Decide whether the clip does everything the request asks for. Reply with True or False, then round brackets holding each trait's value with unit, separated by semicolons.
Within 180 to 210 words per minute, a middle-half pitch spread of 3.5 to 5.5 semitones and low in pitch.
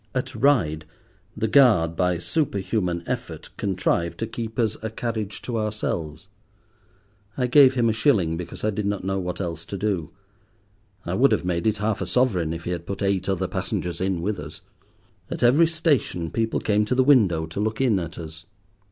True (190 wpm; 4.8 semitones; 100 Hz)